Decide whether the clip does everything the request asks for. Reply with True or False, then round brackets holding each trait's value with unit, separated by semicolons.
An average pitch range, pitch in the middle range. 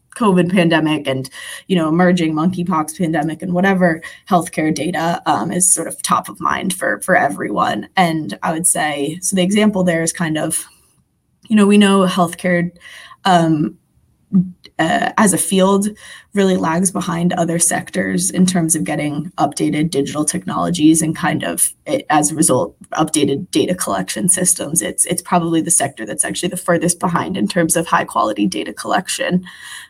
False (2.3 semitones; 175 Hz)